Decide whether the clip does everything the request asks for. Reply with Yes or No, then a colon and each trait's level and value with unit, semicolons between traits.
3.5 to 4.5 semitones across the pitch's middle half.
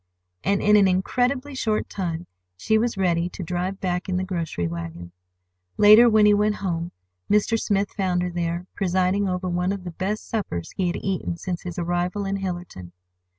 No: average, 2.7 semitones